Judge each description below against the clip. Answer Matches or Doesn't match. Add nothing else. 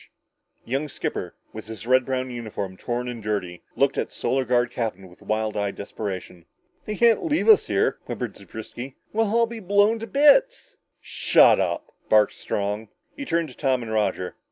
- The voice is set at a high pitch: Doesn't match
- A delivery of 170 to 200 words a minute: Matches